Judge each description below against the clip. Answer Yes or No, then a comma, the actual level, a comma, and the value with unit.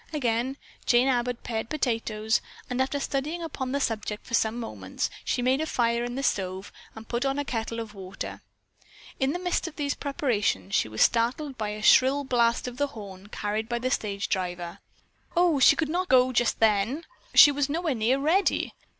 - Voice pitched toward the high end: Yes, high, 245 Hz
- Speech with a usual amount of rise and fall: Yes, average, 4.3 semitones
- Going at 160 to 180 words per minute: No, average, 195 wpm